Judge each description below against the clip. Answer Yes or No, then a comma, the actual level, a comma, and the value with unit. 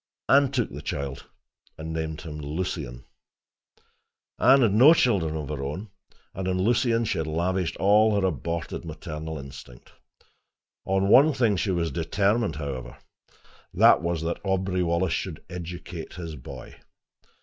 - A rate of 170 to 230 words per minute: No, average, 150 wpm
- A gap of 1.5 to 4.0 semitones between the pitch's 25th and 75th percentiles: No, average, 4.4 semitones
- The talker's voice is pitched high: No, very low, 85 Hz